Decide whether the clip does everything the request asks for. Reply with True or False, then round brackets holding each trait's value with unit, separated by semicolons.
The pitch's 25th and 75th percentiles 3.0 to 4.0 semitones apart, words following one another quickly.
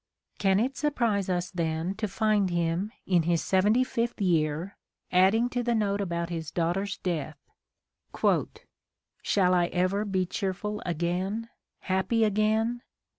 False (3.6 semitones; 135 wpm)